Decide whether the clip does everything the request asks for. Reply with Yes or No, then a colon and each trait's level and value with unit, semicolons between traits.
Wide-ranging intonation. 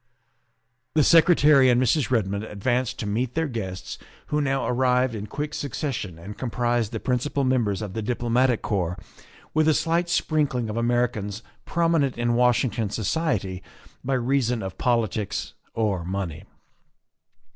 No: average, 4.4 semitones